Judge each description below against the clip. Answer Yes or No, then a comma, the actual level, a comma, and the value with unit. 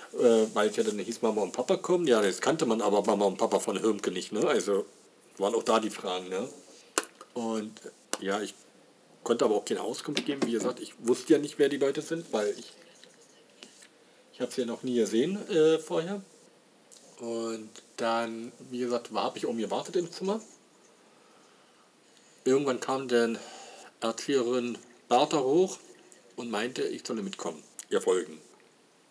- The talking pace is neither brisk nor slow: Yes, average, 170 wpm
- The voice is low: Yes, low, 125 Hz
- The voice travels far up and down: Yes, wide, 5.7 semitones